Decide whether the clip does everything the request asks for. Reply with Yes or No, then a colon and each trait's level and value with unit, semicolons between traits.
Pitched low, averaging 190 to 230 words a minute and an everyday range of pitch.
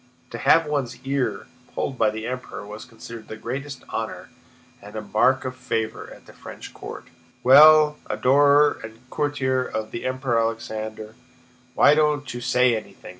No: low, 125 Hz; average, 155 wpm; average, 3.9 semitones